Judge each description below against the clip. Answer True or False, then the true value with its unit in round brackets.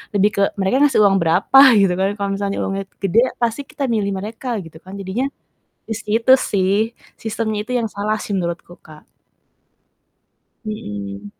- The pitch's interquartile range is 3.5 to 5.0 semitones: False (2.9 semitones)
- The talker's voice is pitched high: True (200 Hz)